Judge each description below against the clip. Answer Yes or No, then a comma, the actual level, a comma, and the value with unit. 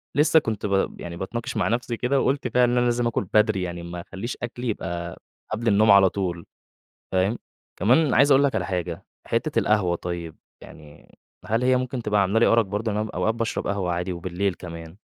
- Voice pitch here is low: Yes, low, 105 Hz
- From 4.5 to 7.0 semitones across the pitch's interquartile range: Yes, average, 4.9 semitones